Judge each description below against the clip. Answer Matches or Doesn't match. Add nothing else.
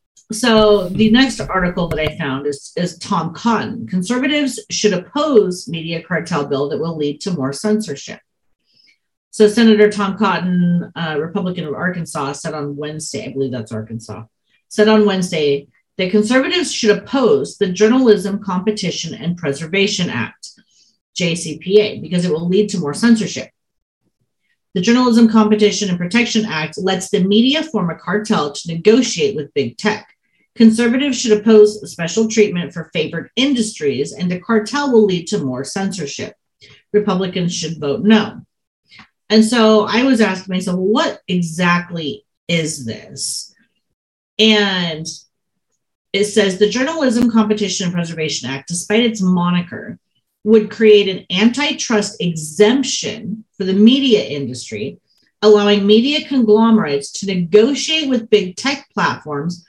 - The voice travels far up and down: Doesn't match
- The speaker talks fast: Doesn't match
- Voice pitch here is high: Matches